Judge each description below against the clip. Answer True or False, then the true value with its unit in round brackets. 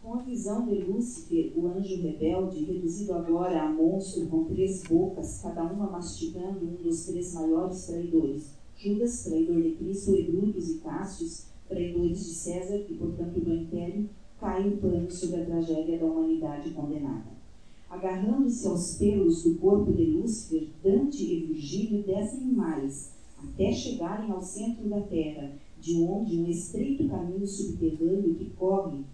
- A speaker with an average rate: True (150 wpm)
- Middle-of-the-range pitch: True (180 Hz)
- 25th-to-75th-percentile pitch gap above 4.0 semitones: False (3.1 semitones)